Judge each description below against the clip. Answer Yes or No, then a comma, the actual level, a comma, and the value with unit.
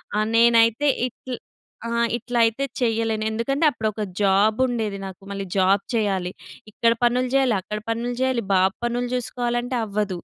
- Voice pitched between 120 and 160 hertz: No, high, 230 Hz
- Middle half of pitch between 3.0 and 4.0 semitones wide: No, narrow, 2.6 semitones